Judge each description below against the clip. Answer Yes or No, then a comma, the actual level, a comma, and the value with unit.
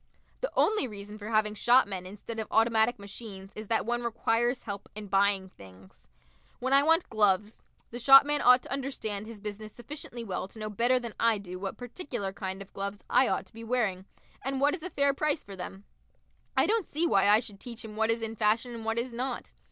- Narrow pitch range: No, average, 3.6 semitones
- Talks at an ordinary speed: No, fast, 215 wpm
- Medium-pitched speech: No, high, 225 Hz